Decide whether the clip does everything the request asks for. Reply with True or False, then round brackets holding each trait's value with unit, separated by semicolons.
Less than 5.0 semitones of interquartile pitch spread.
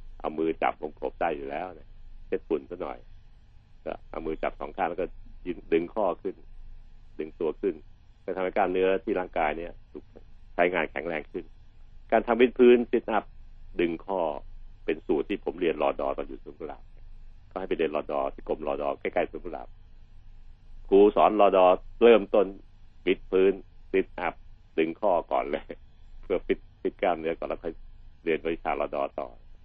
True (4.0 semitones)